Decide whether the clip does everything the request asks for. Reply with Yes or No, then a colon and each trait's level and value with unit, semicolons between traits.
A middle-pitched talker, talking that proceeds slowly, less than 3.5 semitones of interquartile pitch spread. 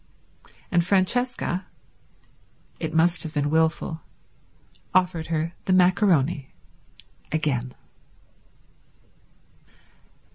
Yes: medium, 165 Hz; slow, 60 wpm; average, 2.8 semitones